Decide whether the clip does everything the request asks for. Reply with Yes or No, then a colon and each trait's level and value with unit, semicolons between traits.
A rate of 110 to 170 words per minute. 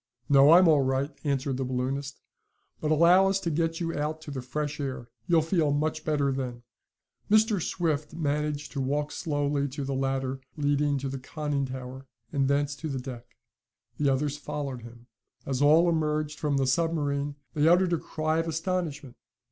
No: average, 180 wpm